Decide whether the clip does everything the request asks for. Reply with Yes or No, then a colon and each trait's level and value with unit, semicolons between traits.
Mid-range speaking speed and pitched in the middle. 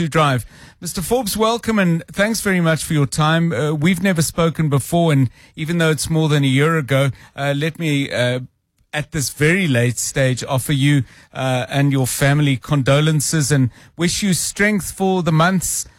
Yes: average, 185 wpm; medium, 150 Hz